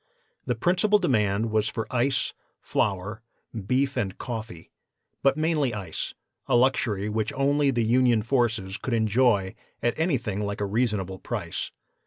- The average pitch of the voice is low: Yes, low, 115 Hz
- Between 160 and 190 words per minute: No, average, 140 wpm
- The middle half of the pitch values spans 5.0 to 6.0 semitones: No, average, 4.1 semitones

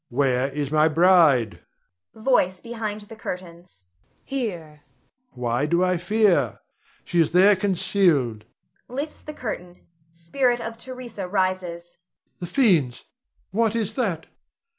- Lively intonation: Yes, wide, 5.9 semitones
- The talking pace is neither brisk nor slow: No, slow, 120 wpm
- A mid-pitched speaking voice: Yes, medium, 180 Hz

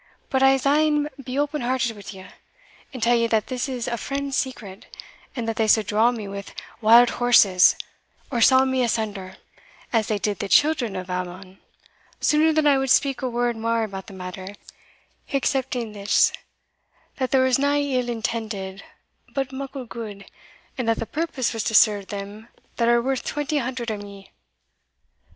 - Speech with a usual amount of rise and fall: Yes, average, 4.3 semitones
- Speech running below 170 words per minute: No, average, 175 wpm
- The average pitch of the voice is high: Yes, high, 235 Hz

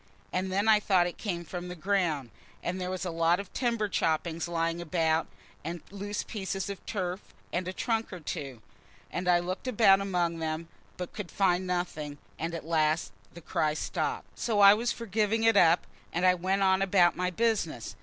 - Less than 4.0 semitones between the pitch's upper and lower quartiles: Yes, average, 3.0 semitones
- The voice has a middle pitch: Yes, medium, 180 Hz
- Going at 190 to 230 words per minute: Yes, average, 195 wpm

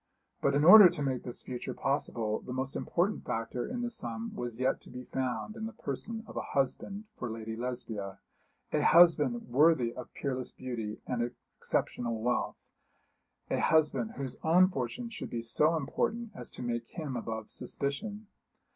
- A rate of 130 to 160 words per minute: No, average, 170 wpm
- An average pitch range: No, wide, 5.7 semitones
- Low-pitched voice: Yes, low, 130 Hz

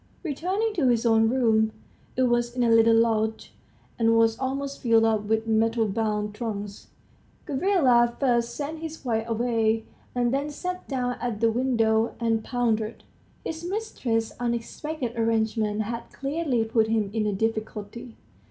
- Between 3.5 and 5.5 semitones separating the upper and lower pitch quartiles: No, average, 2.7 semitones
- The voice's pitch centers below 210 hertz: No, high, 230 Hz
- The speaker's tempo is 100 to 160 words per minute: Yes, average, 150 wpm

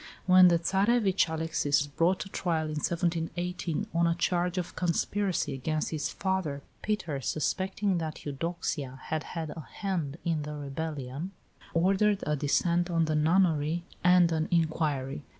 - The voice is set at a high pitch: No, medium, 165 Hz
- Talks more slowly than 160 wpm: Yes, average, 150 wpm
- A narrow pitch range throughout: No, average, 3.1 semitones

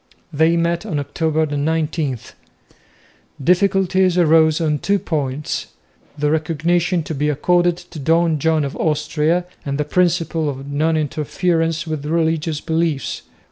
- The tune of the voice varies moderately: No, narrow, 2.2 semitones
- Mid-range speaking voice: Yes, medium, 160 Hz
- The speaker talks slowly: Yes, slow, 130 wpm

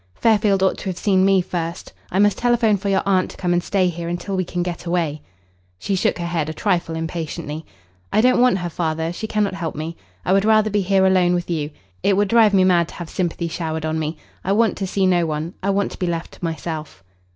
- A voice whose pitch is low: No, medium, 180 Hz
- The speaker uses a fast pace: Yes, fast, 245 wpm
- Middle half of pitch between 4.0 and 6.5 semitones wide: No, average, 2.9 semitones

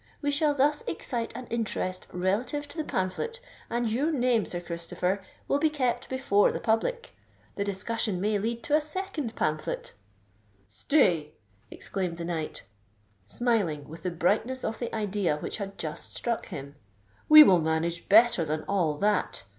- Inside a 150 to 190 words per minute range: Yes, average, 160 wpm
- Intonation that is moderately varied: No, wide, 6.8 semitones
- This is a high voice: Yes, high, 210 Hz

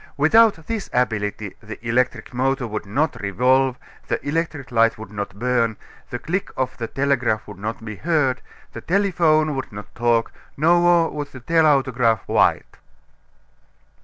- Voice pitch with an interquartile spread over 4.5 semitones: Yes, average, 5.3 semitones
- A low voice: Yes, low, 130 Hz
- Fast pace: No, average, 145 wpm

